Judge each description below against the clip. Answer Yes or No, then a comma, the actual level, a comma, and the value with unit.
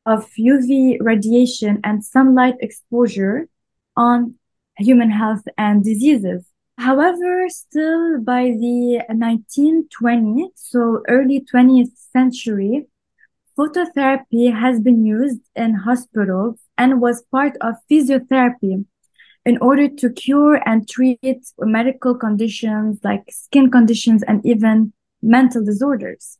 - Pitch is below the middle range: No, high, 245 Hz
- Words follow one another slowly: Yes, slow, 105 wpm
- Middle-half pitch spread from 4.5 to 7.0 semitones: No, average, 2.9 semitones